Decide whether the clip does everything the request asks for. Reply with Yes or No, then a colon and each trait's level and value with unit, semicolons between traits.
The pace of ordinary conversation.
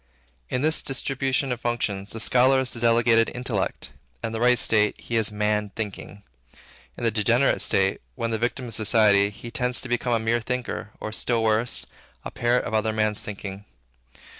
Yes: average, 185 wpm